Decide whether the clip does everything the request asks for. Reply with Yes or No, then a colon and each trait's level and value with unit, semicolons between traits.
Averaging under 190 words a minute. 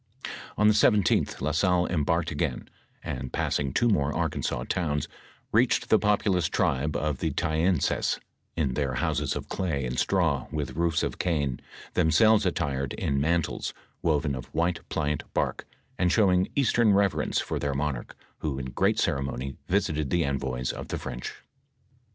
Yes: average, 155 wpm